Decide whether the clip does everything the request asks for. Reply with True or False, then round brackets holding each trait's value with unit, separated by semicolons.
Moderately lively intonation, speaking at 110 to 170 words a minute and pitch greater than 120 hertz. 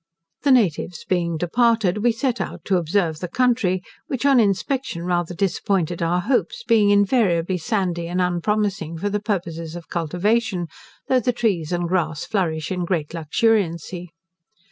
True (4.4 semitones; 150 wpm; 185 Hz)